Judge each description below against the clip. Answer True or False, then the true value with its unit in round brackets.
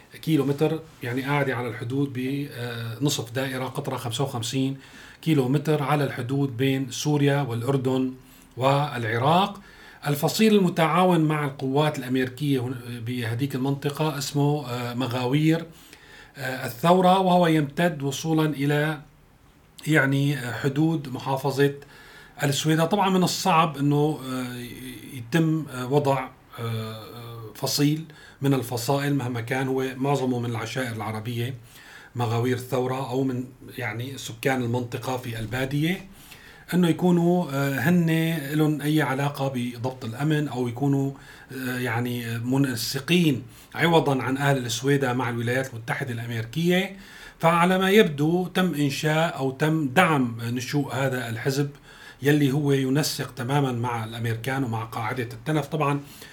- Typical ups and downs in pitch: True (3.1 semitones)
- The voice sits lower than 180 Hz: True (140 Hz)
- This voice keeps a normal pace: True (110 wpm)